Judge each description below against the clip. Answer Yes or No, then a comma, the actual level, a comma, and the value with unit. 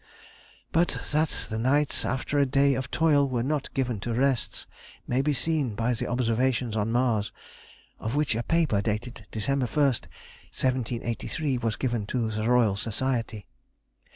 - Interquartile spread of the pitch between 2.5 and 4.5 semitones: Yes, average, 3.4 semitones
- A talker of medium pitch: No, low, 125 Hz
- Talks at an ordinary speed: Yes, average, 155 wpm